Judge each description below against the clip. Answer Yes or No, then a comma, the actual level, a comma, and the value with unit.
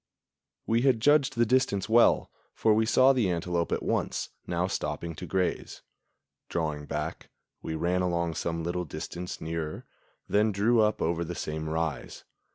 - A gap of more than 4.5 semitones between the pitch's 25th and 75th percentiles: Yes, average, 5.1 semitones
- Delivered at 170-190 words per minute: No, average, 160 wpm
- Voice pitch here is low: Yes, very low, 90 Hz